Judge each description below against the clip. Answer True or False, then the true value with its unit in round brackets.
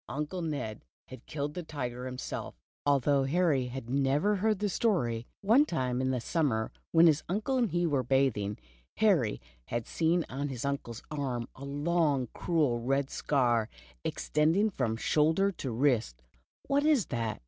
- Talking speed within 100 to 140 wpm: False (160 wpm)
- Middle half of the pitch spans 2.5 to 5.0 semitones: False (5.5 semitones)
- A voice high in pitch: False (140 Hz)